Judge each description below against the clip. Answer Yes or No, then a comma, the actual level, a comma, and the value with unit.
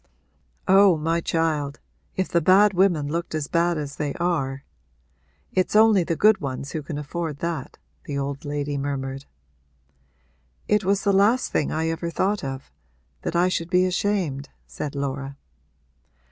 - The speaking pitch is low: No, medium, 165 Hz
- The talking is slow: No, average, 155 wpm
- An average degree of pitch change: Yes, average, 4.5 semitones